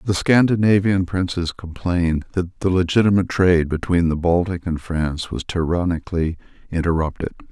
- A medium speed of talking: No, slow, 130 wpm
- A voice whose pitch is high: No, very low, 90 Hz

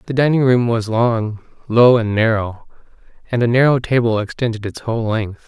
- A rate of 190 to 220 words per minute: No, average, 175 wpm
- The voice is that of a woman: No, male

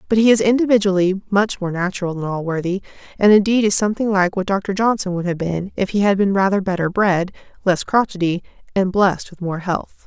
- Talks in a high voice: Yes, high, 195 Hz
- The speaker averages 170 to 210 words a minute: Yes, fast, 205 wpm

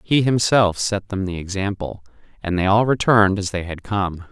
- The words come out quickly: No, average, 195 wpm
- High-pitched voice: No, low, 100 Hz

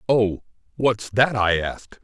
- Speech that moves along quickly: No, average, 145 wpm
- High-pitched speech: No, low, 110 Hz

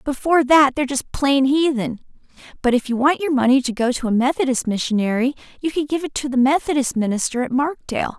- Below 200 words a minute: No, fast, 205 wpm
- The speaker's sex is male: No, female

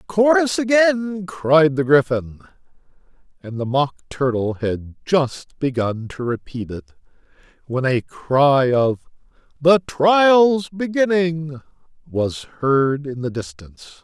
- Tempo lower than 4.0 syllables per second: Yes, 3.4 syllables/s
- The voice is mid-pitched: Yes, medium, 150 Hz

